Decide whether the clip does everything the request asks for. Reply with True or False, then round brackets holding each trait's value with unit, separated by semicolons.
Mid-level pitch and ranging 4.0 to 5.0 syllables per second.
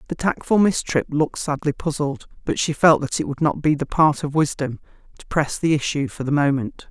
False (150 Hz; 5.4 syllables/s)